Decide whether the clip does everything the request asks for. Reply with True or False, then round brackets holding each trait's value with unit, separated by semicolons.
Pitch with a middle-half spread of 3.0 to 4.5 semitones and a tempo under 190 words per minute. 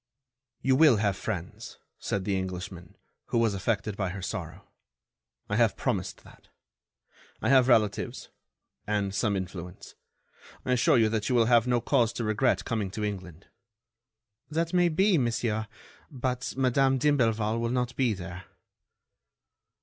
True (4.2 semitones; 145 wpm)